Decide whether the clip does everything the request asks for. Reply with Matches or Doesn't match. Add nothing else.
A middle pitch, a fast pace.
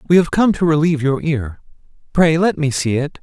Matches